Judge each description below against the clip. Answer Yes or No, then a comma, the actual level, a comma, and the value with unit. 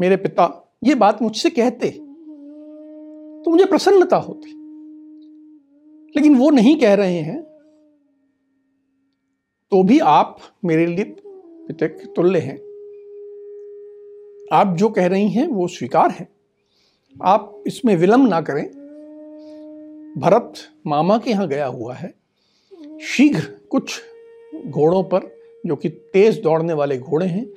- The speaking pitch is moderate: No, very high, 290 Hz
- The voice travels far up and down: Yes, wide, 6.9 semitones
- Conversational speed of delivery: Yes, average, 120 wpm